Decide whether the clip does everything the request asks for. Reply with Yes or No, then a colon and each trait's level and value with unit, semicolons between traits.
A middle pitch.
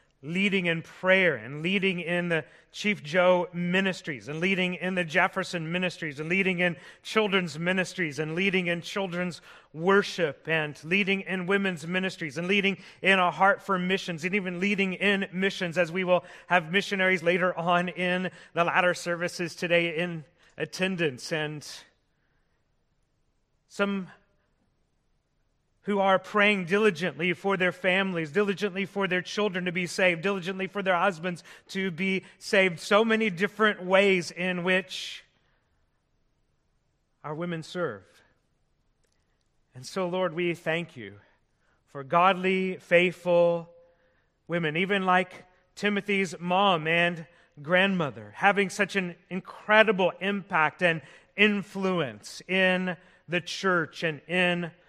Yes: medium, 180 Hz